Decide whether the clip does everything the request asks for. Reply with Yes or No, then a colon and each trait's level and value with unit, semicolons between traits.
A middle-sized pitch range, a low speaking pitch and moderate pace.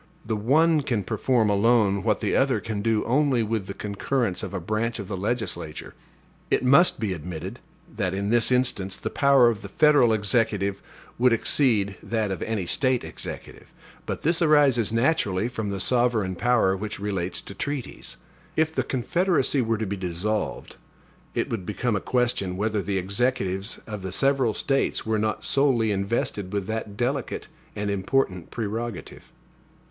Yes: average, 4.0 semitones; low, 110 Hz; average, 165 wpm